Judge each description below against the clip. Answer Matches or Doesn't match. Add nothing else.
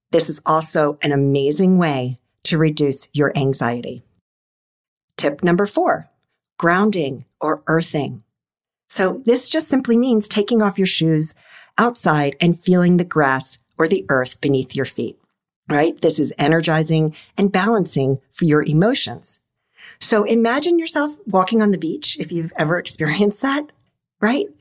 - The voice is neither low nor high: Matches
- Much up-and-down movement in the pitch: Matches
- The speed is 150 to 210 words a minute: Doesn't match